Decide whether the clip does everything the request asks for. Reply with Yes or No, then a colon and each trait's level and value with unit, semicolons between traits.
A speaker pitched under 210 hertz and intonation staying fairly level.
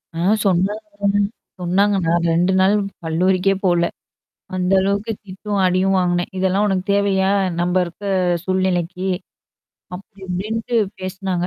Yes: high, 190 Hz; narrow, 1.8 semitones